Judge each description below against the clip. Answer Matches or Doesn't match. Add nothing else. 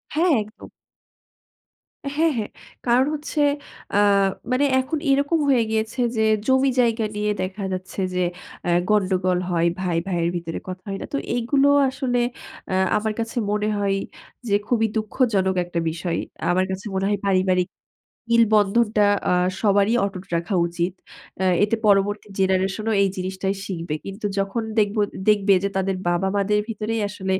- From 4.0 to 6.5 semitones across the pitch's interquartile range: Doesn't match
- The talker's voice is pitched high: Matches